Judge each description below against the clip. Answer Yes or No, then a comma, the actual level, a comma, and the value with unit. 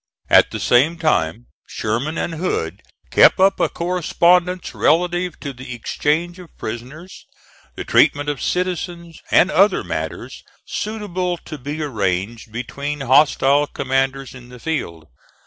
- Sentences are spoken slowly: Yes, slow, 130 wpm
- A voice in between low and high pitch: Yes, medium, 150 Hz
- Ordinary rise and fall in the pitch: No, wide, 5.8 semitones